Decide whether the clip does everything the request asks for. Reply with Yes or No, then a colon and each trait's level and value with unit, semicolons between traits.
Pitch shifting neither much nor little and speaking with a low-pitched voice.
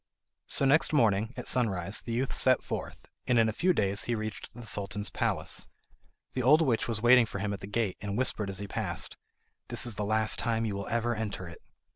Yes: average, 3.0 semitones; low, 110 Hz